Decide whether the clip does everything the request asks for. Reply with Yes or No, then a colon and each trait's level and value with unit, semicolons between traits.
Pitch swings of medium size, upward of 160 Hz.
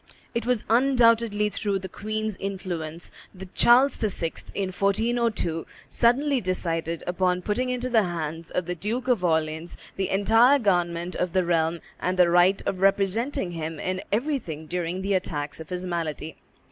Yes: average, 4.7 semitones; medium, 185 Hz